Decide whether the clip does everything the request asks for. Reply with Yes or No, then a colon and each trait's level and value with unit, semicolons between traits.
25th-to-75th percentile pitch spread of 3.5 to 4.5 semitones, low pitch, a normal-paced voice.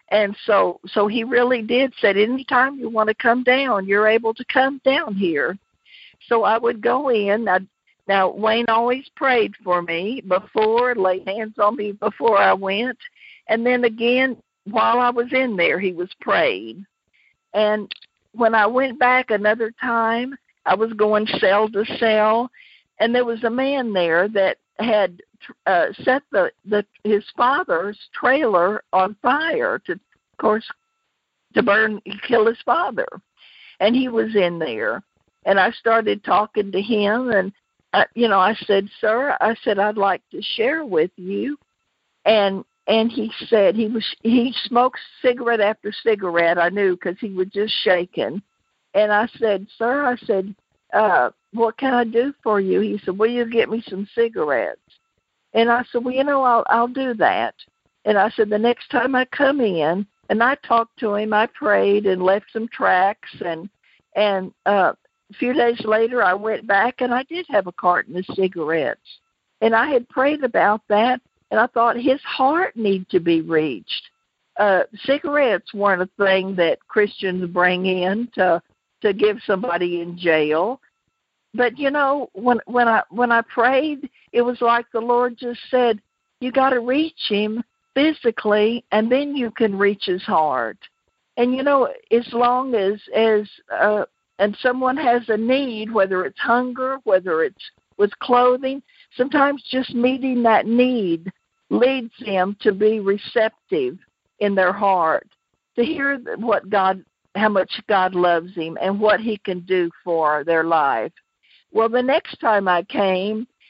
No: average, 3.8 semitones; high, 225 Hz; average, 165 wpm